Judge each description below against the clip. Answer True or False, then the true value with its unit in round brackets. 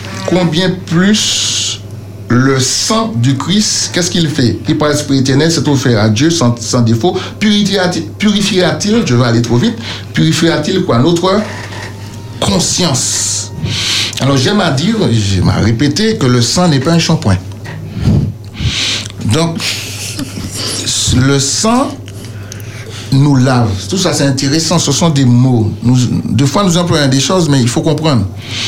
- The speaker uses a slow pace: True (140 wpm)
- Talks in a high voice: False (130 Hz)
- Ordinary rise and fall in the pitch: False (7.1 semitones)